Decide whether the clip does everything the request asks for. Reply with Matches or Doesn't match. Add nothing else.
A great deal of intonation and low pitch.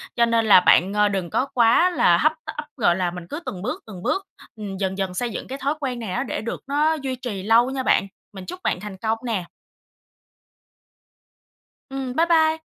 Doesn't match